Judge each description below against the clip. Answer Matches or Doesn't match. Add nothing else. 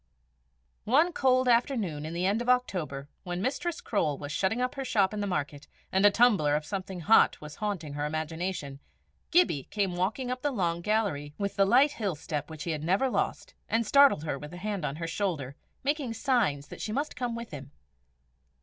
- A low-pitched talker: Doesn't match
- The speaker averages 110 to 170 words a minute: Doesn't match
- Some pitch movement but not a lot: Doesn't match